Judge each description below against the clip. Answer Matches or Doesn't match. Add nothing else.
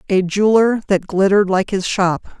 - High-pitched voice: Matches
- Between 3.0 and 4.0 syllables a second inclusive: Doesn't match